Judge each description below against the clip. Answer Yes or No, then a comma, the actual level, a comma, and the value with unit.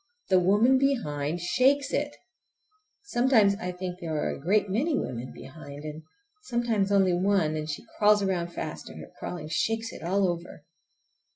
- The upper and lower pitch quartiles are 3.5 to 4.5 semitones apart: No, average, 5.1 semitones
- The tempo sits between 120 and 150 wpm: No, average, 165 wpm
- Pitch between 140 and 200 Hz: Yes, high, 190 Hz